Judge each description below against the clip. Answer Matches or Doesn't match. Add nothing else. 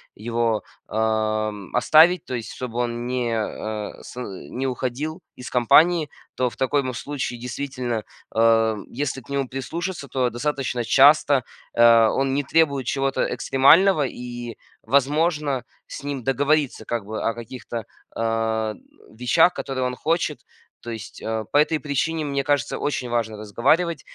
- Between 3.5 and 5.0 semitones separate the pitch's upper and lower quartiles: Matches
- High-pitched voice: Doesn't match